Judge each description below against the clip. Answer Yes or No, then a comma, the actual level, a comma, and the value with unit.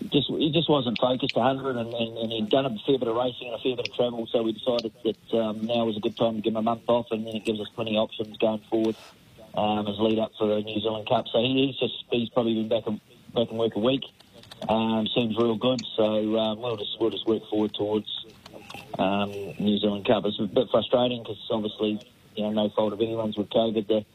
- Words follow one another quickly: Yes, fast, 255 wpm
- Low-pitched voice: Yes, low, 115 Hz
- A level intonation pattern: Yes, narrow, 2.1 semitones